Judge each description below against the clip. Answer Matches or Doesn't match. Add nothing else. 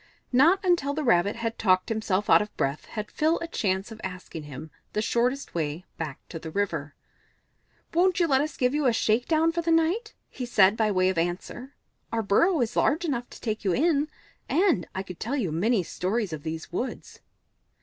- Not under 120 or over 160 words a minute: Doesn't match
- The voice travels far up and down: Matches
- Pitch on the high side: Matches